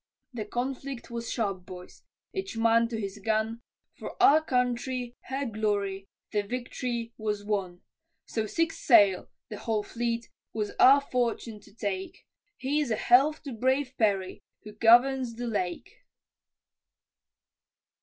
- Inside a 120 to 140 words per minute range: Yes, slow, 135 wpm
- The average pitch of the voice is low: No, high, 230 Hz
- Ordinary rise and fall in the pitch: Yes, average, 3.3 semitones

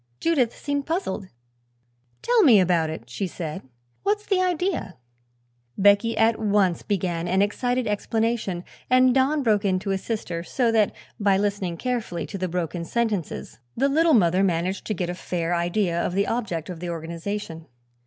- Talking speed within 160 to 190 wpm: Yes, average, 165 wpm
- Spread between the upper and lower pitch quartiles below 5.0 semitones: No, average, 5.3 semitones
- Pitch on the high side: Yes, high, 200 Hz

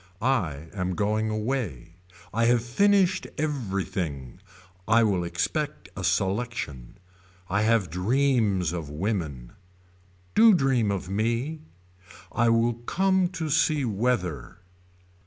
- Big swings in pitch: Yes, wide, 6.3 semitones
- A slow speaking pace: Yes, slow, 110 wpm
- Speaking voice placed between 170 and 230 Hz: No, low, 110 Hz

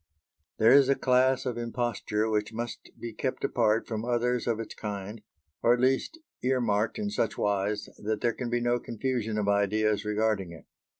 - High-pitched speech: No, low, 115 Hz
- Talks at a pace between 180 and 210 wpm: Yes, average, 185 wpm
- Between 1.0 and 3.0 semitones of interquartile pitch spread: Yes, narrow, 2.6 semitones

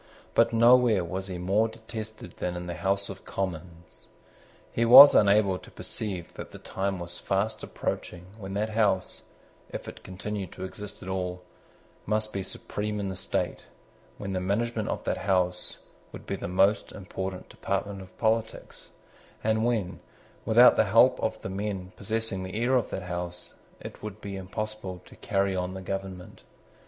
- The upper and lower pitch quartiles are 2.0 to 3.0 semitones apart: Yes, narrow, 2.6 semitones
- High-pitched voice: No, very low, 95 Hz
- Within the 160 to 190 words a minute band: Yes, average, 165 wpm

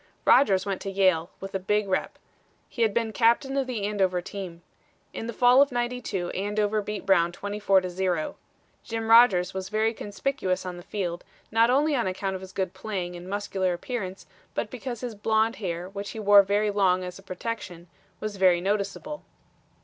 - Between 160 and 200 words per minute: Yes, average, 190 wpm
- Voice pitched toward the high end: Yes, high, 200 Hz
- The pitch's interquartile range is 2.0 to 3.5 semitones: Yes, average, 3.2 semitones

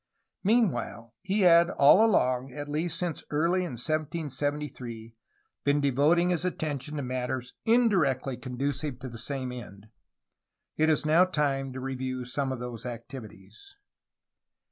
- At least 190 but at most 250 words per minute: No, average, 140 wpm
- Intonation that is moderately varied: Yes, average, 4.8 semitones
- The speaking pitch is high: No, medium, 140 Hz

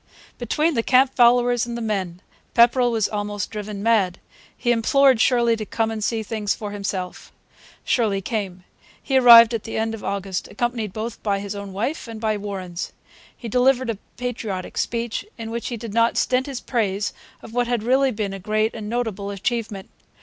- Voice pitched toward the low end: No, high, 225 Hz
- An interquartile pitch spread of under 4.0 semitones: Yes, average, 2.9 semitones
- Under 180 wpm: No, average, 185 wpm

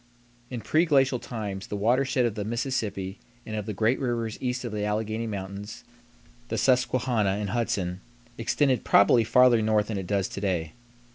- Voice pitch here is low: Yes, low, 110 Hz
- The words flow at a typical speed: Yes, average, 165 wpm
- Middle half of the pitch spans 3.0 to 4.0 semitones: Yes, average, 3.4 semitones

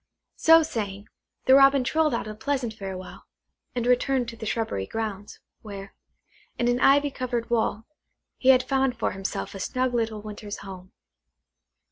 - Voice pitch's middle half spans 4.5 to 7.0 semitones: No, average, 3.9 semitones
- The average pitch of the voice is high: Yes, high, 230 Hz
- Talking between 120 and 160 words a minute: Yes, average, 155 wpm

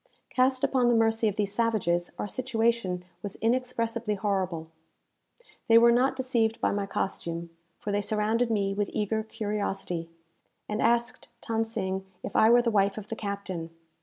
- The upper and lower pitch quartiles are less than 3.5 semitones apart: Yes, average, 2.8 semitones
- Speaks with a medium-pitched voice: No, high, 215 Hz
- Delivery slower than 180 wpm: Yes, average, 165 wpm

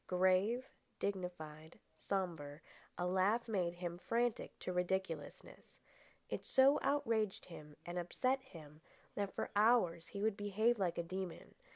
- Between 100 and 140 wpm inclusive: Yes, slow, 135 wpm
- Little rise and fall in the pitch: No, average, 4.1 semitones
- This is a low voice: No, medium, 185 Hz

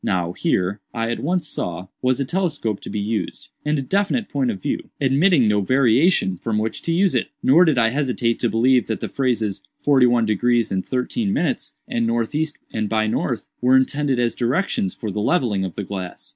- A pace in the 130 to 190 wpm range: No, fast, 205 wpm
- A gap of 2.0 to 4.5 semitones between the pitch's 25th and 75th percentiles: No, average, 4.9 semitones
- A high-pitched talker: No, low, 120 Hz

